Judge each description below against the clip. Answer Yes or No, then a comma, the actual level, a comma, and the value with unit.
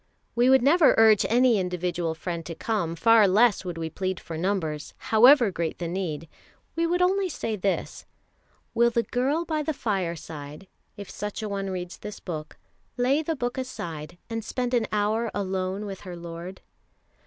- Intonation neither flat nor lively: No, wide, 5.8 semitones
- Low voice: No, high, 200 Hz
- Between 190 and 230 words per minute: No, average, 175 wpm